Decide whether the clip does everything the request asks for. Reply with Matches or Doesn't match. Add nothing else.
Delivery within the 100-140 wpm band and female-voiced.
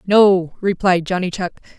Matches